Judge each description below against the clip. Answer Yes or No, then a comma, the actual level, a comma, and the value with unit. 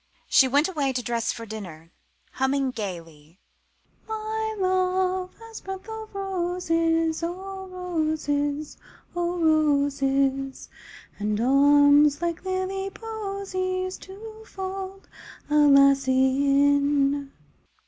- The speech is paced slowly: Yes, slow, 95 wpm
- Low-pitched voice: No, very high, 315 Hz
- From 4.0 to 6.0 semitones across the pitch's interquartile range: Yes, wide, 5.4 semitones